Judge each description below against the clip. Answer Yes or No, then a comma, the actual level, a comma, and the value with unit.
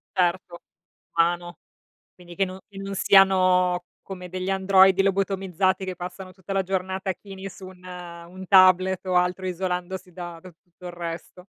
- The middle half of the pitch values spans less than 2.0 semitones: Yes, narrow, 1.2 semitones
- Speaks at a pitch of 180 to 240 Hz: Yes, medium, 185 Hz